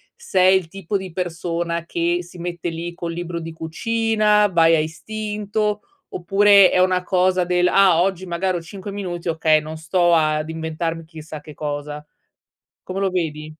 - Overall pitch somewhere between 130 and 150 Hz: No, medium, 175 Hz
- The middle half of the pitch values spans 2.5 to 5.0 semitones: Yes, average, 2.8 semitones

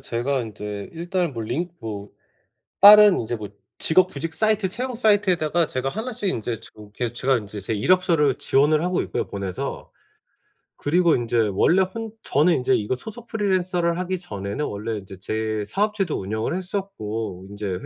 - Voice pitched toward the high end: No, medium, 145 Hz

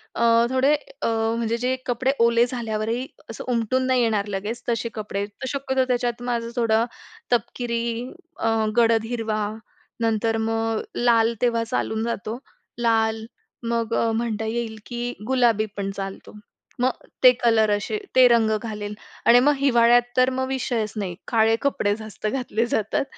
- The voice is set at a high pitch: Yes, high, 230 Hz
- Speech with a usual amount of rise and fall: No, narrow, 1.7 semitones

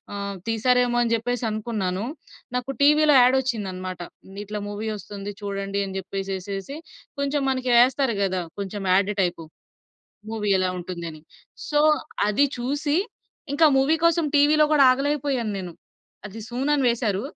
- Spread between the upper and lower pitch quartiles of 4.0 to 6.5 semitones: Yes, wide, 5.4 semitones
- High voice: Yes, high, 225 Hz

